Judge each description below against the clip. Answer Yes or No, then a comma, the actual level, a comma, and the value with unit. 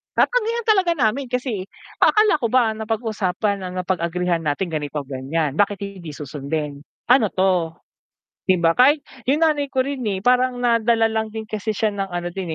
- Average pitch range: No, wide, 6.4 semitones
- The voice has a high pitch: Yes, high, 210 Hz